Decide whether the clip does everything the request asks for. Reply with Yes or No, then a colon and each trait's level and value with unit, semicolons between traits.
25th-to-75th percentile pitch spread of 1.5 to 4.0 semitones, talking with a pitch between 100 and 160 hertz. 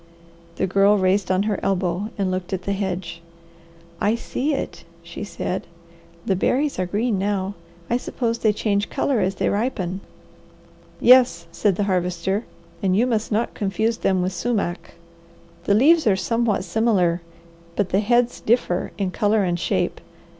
No: average, 3.3 semitones; high, 200 Hz